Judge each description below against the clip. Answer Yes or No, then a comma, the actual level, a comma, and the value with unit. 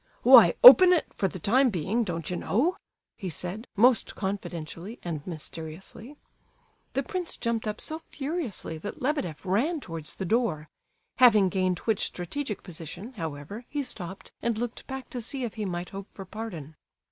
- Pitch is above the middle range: Yes, high, 205 Hz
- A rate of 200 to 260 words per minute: No, average, 165 wpm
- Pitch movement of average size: No, wide, 6.0 semitones